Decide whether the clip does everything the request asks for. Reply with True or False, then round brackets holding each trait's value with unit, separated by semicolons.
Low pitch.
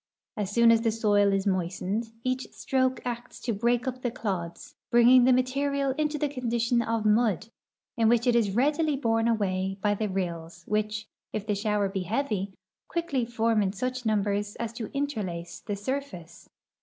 False (225 Hz)